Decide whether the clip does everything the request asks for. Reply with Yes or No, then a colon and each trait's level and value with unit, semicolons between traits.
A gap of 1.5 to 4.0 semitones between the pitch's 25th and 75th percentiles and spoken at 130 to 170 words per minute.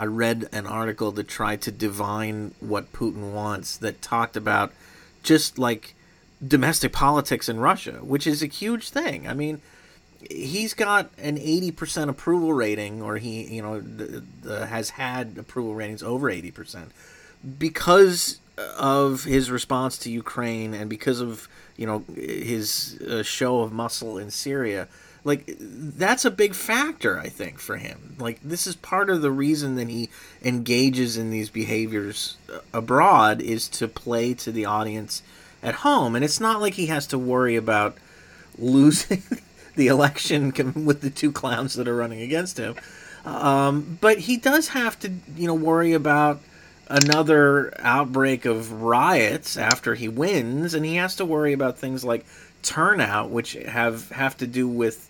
No: average, 5.2 semitones; average, 160 wpm